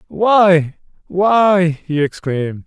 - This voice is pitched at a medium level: Yes, medium, 175 Hz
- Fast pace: No, slow, 70 wpm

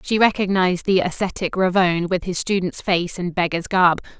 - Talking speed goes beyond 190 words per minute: No, average, 170 wpm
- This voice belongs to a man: No, female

